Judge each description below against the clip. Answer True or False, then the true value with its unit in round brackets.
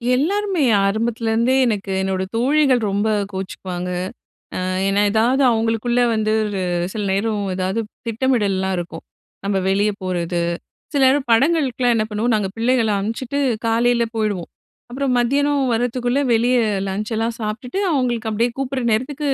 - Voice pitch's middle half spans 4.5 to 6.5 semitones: False (3.7 semitones)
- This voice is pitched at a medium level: False (230 Hz)